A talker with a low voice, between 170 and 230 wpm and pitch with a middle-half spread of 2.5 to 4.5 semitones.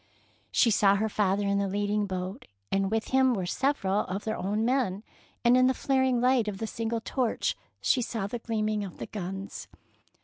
No: high, 215 Hz; average, 200 wpm; average, 3.4 semitones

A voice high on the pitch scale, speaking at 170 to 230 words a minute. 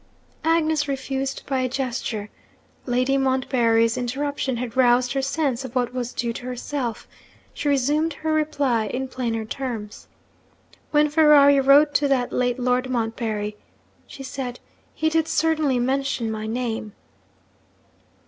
No: very high, 260 Hz; slow, 135 wpm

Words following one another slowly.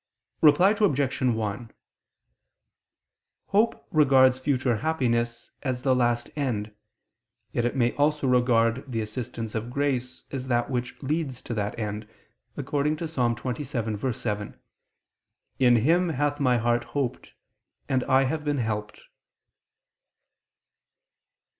Yes: slow, 115 wpm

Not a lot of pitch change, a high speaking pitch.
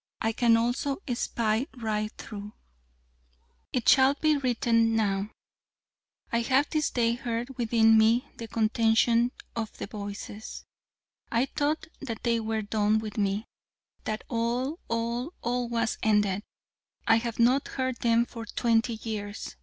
Yes: narrow, 1.9 semitones; high, 230 Hz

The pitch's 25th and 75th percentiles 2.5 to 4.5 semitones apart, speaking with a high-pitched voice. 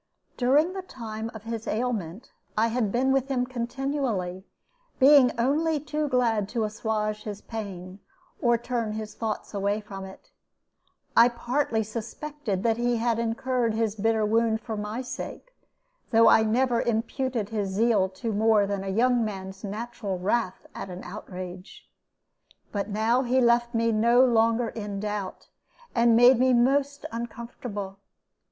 Yes: average, 2.9 semitones; high, 225 Hz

